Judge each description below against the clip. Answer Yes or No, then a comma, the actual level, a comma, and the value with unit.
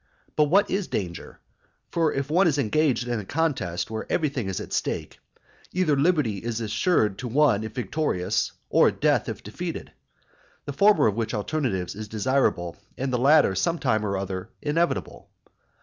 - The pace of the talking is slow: No, average, 165 wpm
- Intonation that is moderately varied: No, wide, 6.6 semitones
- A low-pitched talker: Yes, low, 125 Hz